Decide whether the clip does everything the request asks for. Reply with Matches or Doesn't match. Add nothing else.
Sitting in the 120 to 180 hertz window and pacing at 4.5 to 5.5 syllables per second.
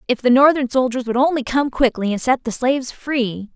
Doesn't match